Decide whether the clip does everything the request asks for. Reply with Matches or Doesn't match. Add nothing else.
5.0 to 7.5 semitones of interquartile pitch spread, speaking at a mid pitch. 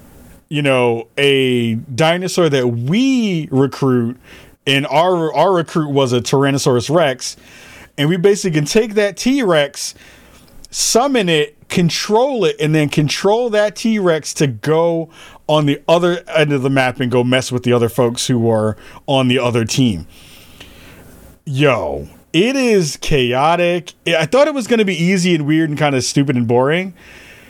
Matches